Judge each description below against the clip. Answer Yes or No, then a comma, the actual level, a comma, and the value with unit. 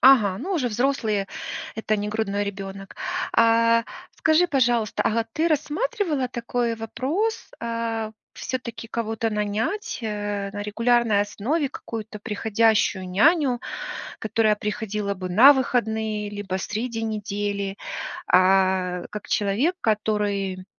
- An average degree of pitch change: Yes, average, 3.0 semitones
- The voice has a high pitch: Yes, high, 220 Hz